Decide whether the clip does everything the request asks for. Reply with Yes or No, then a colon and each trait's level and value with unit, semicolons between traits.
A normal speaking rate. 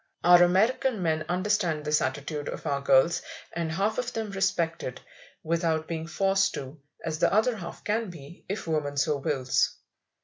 Yes: average, 170 wpm